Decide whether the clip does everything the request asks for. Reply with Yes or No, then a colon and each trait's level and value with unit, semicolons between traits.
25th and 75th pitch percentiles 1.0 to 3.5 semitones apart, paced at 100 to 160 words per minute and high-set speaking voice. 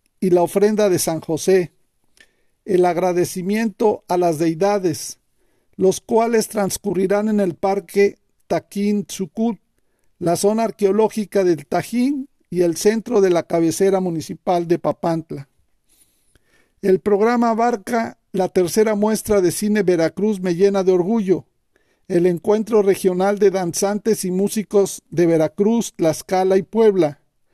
Yes: average, 3.2 semitones; slow, 125 wpm; high, 195 Hz